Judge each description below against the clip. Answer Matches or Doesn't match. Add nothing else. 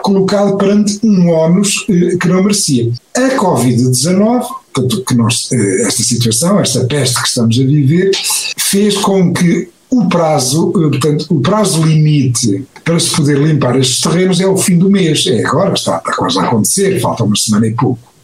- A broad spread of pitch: Matches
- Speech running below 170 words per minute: Doesn't match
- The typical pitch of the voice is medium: Matches